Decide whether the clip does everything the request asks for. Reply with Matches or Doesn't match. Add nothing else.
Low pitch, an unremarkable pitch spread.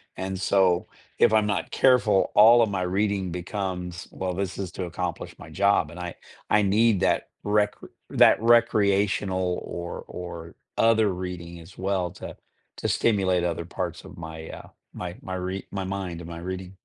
Doesn't match